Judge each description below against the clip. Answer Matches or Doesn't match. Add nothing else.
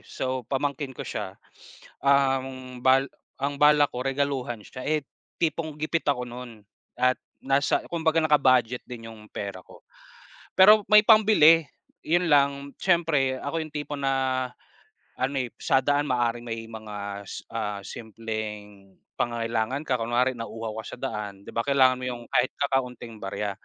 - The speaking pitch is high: Doesn't match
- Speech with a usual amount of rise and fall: Matches